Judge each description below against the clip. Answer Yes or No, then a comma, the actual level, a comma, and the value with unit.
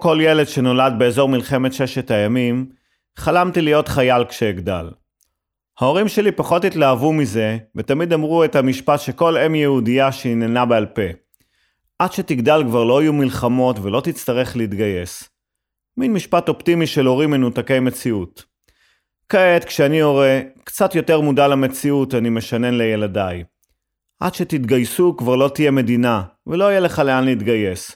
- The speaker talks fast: No, average, 135 wpm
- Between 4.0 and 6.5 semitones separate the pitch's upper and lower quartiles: Yes, average, 4.5 semitones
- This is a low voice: Yes, low, 130 Hz